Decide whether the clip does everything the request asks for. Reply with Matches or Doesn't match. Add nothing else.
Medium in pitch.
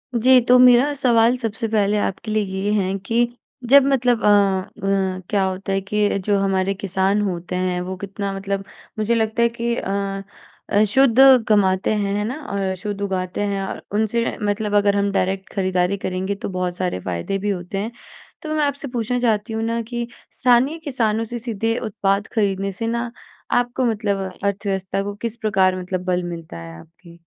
Doesn't match